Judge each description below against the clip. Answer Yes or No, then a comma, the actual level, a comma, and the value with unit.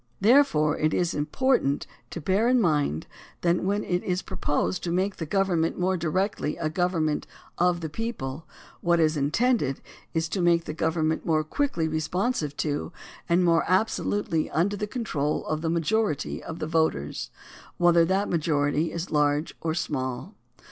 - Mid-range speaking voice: Yes, medium, 170 Hz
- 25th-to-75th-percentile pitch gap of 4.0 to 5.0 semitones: No, average, 3.5 semitones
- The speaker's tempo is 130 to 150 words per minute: No, average, 160 wpm